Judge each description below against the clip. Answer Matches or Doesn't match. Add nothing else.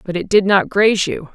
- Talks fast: Matches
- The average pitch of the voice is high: Matches